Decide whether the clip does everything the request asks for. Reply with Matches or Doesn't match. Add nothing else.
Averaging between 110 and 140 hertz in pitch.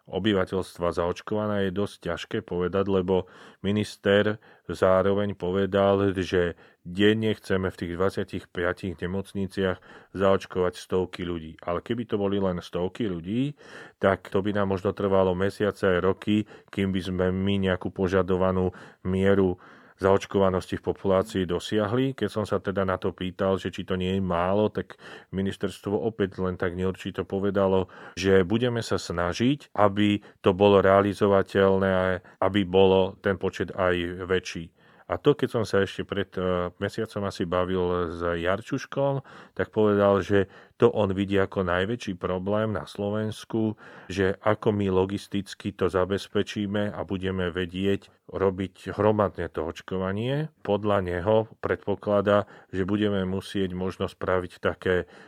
Doesn't match